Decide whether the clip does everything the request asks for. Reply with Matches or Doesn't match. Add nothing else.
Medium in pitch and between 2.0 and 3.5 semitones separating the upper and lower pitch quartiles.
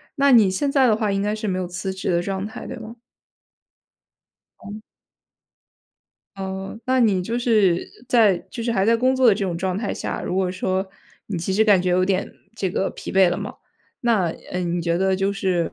Doesn't match